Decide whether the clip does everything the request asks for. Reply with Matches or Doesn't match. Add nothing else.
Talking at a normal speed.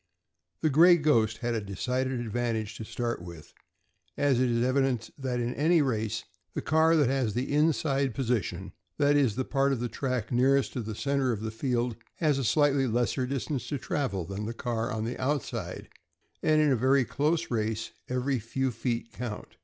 Matches